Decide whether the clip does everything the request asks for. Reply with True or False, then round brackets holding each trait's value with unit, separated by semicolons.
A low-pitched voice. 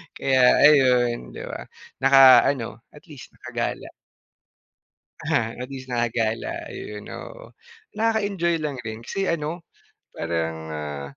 True (125 Hz)